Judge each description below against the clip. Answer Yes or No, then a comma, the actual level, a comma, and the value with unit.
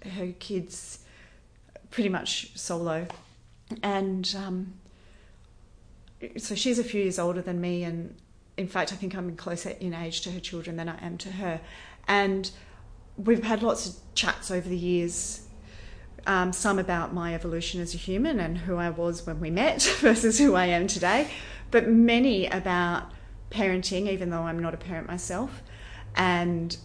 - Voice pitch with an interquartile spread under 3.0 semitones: Yes, narrow, 2.5 semitones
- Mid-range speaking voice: Yes, medium, 180 Hz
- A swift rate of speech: No, average, 165 wpm